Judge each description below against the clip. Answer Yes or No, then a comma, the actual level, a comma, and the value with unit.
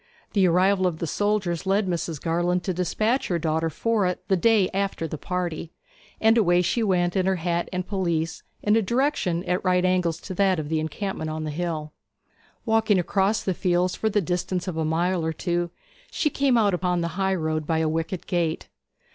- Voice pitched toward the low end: No, medium, 180 Hz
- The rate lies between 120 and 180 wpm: No, fast, 205 wpm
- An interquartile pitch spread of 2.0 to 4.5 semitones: Yes, average, 2.9 semitones